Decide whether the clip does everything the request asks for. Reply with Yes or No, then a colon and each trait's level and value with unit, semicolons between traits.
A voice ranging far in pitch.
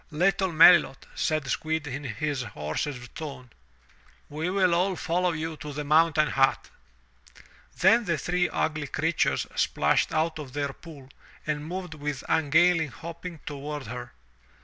No: average, 3.0 semitones